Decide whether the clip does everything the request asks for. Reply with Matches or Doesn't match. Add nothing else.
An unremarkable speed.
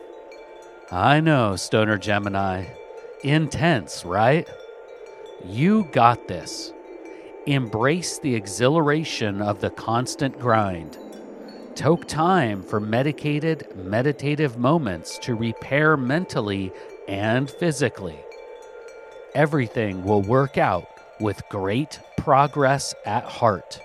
Doesn't match